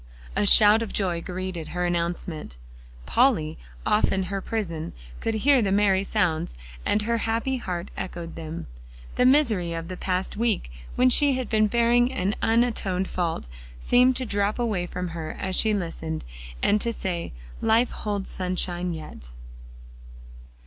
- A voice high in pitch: Yes, high, 195 Hz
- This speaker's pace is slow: No, average, 155 wpm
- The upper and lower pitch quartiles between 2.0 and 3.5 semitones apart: No, average, 4.6 semitones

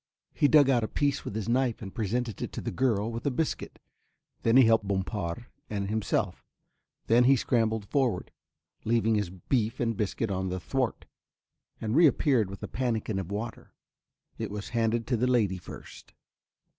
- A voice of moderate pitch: No, low, 115 Hz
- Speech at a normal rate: Yes, average, 175 wpm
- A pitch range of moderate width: Yes, average, 3.3 semitones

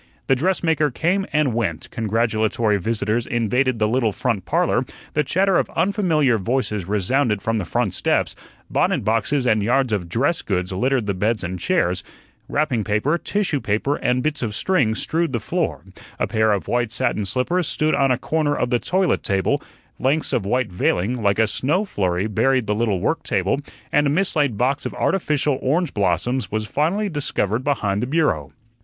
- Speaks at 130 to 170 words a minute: No, average, 180 wpm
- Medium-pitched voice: No, low, 125 Hz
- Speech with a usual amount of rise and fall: No, wide, 5.8 semitones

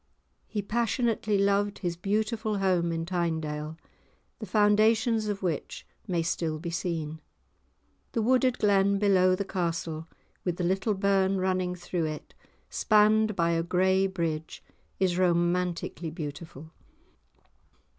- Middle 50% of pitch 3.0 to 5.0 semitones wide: Yes, average, 3.5 semitones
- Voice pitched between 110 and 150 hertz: No, medium, 185 Hz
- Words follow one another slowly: Yes, slow, 125 wpm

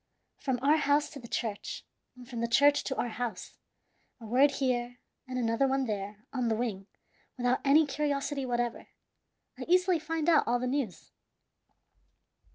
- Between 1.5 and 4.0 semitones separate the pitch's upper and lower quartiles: Yes, average, 3.4 semitones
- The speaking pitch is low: No, very high, 255 Hz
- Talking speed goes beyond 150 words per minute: Yes, average, 165 wpm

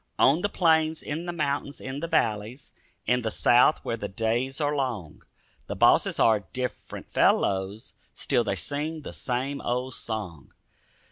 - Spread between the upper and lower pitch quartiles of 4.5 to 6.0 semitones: Yes, average, 4.8 semitones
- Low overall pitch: Yes, low, 125 Hz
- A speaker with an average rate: Yes, average, 155 wpm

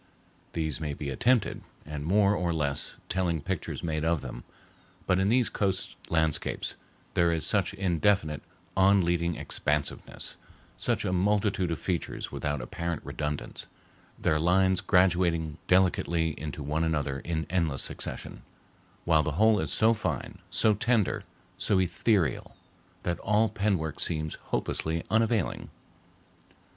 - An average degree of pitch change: Yes, average, 3.7 semitones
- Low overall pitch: Yes, very low, 85 Hz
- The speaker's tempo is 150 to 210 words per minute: No, slow, 135 wpm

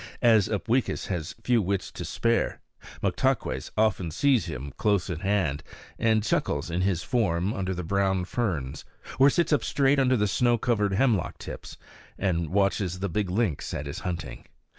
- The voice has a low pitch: Yes, low, 100 Hz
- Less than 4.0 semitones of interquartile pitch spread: No, average, 4.7 semitones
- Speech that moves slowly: No, average, 165 wpm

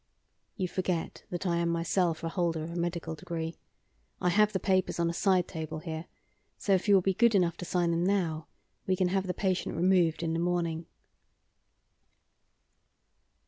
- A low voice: No, medium, 175 Hz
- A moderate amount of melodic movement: No, narrow, 2.1 semitones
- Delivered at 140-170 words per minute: No, average, 185 wpm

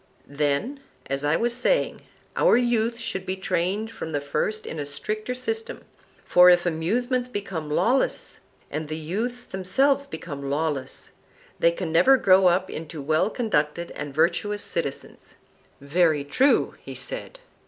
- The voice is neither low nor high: Yes, medium, 180 Hz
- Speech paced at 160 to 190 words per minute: No, average, 145 wpm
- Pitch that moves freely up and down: Yes, wide, 7.2 semitones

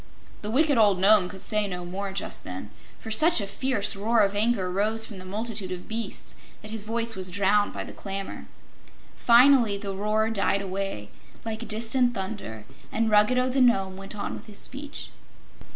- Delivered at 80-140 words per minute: No, average, 185 wpm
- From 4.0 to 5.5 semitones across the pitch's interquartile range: No, average, 2.7 semitones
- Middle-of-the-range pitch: No, high, 210 Hz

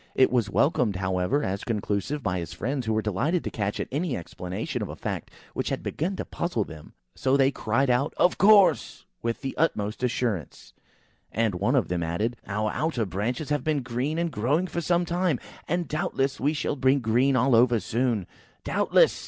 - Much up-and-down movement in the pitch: Yes, wide, 5.8 semitones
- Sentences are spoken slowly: No, average, 195 wpm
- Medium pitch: No, low, 125 Hz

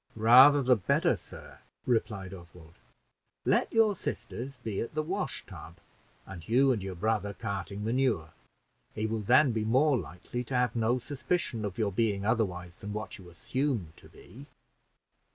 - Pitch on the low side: Yes, low, 110 Hz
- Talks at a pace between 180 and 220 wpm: No, average, 160 wpm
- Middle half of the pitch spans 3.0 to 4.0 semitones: No, average, 4.7 semitones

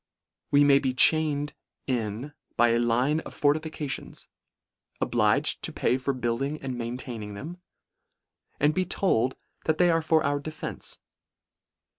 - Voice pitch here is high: No, medium, 140 Hz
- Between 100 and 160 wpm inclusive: Yes, slow, 135 wpm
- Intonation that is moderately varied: Yes, average, 4.2 semitones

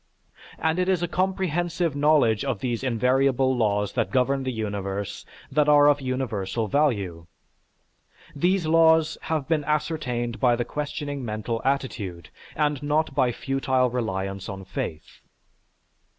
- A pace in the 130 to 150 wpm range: Yes, slow, 135 wpm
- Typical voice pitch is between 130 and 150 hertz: Yes, low, 135 Hz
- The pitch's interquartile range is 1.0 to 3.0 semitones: No, average, 5.1 semitones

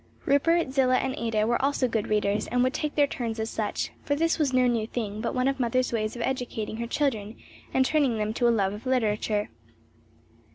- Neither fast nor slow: No, fast, 220 wpm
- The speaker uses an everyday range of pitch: Yes, average, 3.4 semitones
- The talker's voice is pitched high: Yes, high, 240 Hz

